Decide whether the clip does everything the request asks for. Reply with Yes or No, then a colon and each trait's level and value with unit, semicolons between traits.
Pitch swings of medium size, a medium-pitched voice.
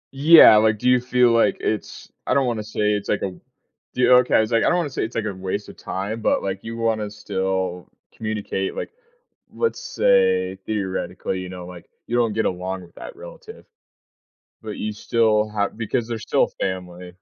No: average, 4.0 semitones; low, 110 Hz